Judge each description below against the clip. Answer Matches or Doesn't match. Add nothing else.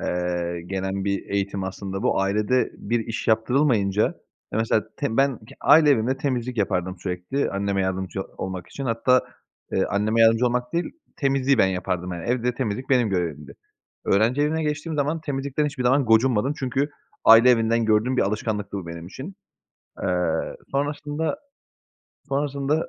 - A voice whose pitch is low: Matches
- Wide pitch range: Matches